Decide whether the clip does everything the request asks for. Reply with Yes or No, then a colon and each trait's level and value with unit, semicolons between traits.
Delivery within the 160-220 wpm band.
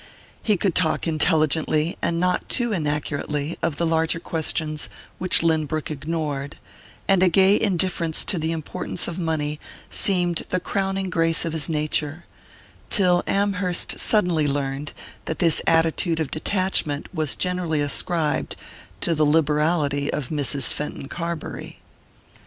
No: slow, 135 wpm